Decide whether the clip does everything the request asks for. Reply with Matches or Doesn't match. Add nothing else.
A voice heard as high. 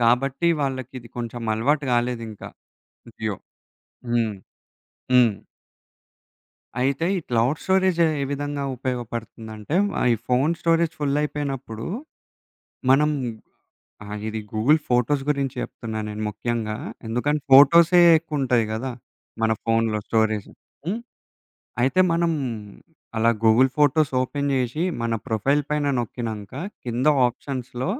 Doesn't match